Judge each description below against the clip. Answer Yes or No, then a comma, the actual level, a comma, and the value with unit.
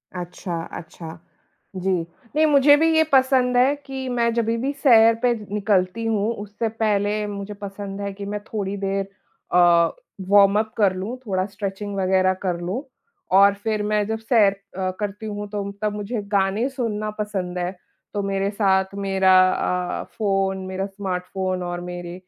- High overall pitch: Yes, high, 200 Hz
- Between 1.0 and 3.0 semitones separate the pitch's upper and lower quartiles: Yes, narrow, 2.6 semitones